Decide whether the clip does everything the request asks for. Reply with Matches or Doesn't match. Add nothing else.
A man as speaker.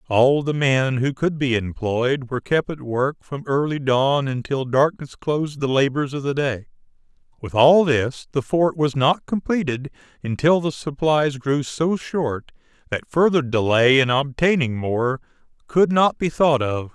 Matches